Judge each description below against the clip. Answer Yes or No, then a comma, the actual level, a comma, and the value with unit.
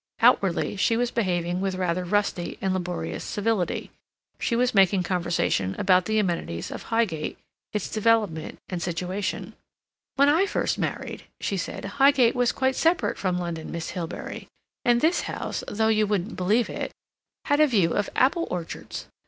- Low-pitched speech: No, high, 200 Hz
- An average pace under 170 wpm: Yes, average, 160 wpm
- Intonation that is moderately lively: Yes, average, 4.6 semitones